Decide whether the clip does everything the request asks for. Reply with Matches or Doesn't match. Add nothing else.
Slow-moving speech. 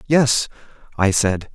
Matches